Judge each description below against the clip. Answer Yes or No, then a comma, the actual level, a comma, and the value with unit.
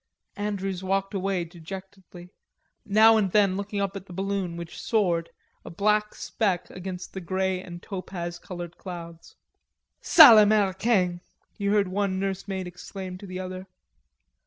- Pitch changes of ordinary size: No, narrow, 1.9 semitones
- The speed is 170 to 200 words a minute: No, average, 140 wpm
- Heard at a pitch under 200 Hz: Yes, high, 190 Hz